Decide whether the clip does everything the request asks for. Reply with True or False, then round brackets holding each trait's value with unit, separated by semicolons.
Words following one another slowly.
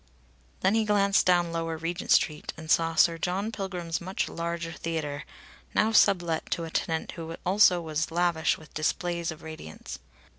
False (160 wpm)